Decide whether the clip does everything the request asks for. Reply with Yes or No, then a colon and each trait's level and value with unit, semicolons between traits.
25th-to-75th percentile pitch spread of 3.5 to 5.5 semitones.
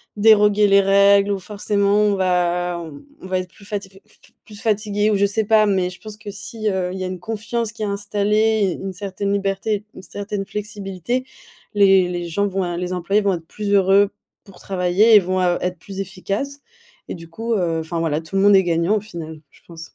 No: narrow, 2.4 semitones